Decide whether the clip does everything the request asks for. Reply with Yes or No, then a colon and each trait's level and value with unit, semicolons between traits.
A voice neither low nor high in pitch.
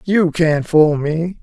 Yes: medium, 165 Hz